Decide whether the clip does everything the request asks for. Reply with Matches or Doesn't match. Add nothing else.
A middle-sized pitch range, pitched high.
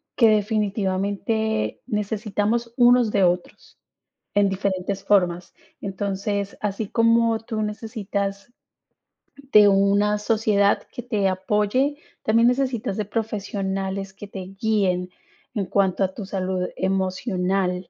Doesn't match